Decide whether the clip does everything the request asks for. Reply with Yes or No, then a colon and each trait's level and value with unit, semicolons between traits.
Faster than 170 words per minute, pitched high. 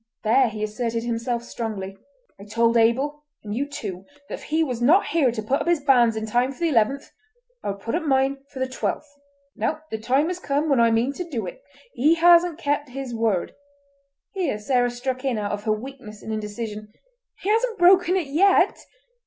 Yes: average, 200 wpm; very high, 260 Hz